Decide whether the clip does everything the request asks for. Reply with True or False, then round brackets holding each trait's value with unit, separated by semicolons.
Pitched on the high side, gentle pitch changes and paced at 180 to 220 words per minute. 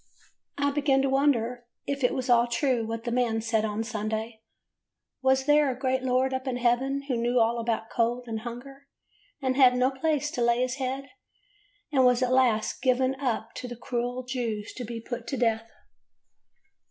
True (250 Hz; 2.2 semitones; 190 wpm)